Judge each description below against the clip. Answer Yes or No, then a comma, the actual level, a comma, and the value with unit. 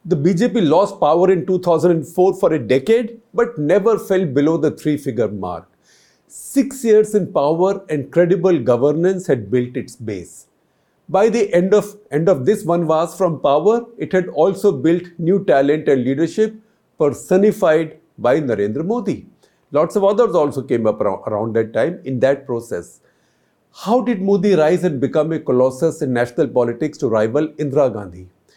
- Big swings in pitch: Yes, wide, 6.0 semitones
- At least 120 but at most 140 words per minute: No, average, 165 wpm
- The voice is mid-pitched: Yes, medium, 165 Hz